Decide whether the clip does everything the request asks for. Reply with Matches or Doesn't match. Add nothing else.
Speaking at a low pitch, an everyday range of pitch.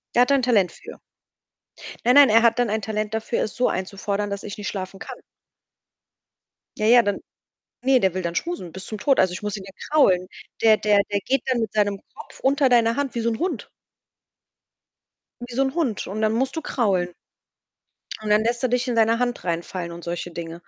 Doesn't match